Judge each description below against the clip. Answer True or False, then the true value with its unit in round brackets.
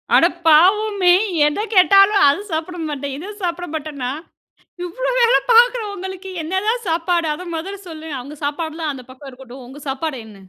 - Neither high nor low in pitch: False (330 Hz)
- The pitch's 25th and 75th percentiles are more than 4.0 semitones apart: True (5.1 semitones)